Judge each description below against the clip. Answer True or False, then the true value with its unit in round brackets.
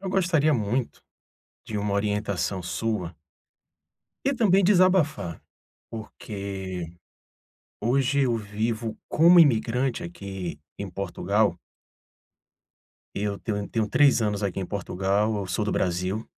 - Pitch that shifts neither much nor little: True (5.0 semitones)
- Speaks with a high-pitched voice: False (105 Hz)